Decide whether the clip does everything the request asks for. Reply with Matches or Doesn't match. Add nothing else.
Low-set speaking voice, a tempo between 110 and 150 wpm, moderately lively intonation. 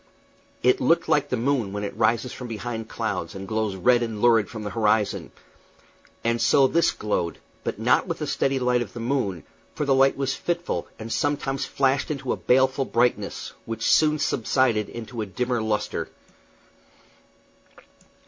Doesn't match